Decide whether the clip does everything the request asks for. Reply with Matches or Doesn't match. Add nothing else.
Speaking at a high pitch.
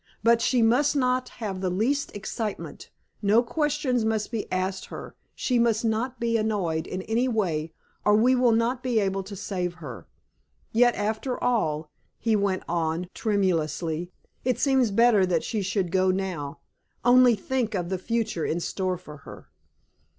Matches